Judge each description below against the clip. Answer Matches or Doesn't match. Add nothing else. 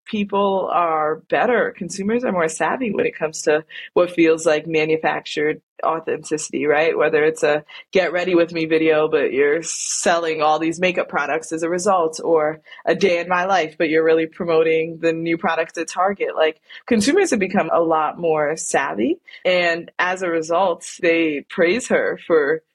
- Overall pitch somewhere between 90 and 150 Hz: Doesn't match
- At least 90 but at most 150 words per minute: Doesn't match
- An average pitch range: Matches